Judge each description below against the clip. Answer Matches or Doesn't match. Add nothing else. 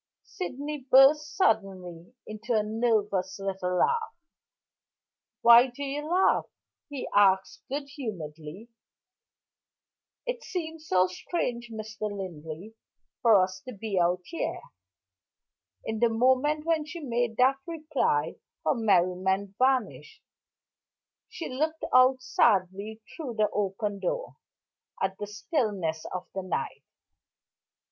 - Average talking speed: Doesn't match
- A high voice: Matches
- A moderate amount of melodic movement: Doesn't match